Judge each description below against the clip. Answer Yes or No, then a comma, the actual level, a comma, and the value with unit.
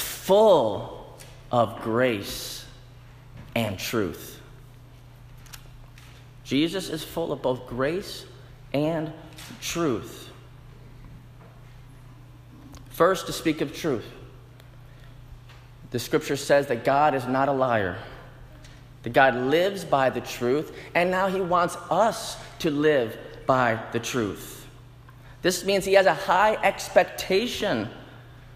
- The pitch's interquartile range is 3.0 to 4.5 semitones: Yes, average, 3.4 semitones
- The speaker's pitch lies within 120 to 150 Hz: Yes, low, 130 Hz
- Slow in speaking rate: Yes, slow, 105 wpm